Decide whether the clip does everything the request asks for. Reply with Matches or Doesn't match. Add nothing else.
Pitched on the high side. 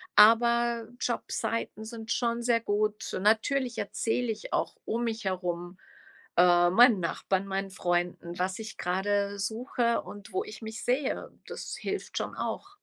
Matches